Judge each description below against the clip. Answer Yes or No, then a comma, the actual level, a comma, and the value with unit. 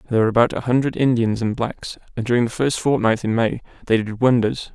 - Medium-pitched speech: No, low, 120 Hz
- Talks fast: Yes, fast, 230 wpm